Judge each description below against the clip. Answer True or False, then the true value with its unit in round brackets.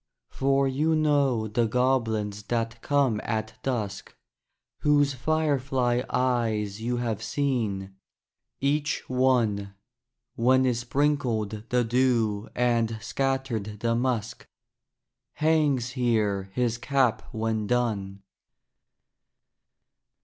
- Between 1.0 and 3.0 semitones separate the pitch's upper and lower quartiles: False (3.4 semitones)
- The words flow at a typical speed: False (95 wpm)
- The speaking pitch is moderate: False (120 Hz)